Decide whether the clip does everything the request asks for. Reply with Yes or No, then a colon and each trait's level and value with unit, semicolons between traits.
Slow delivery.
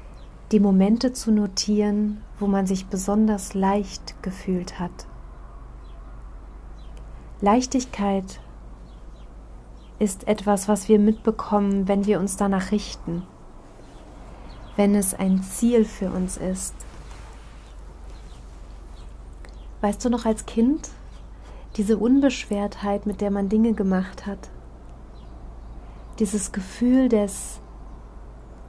Yes: slow, 95 wpm